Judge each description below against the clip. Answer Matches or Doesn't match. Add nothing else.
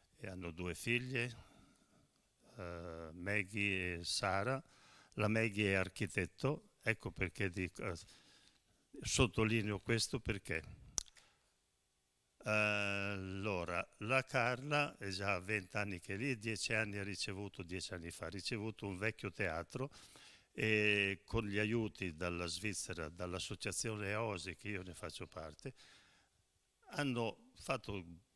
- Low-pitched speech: Matches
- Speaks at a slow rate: Matches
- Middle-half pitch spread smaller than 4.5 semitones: Matches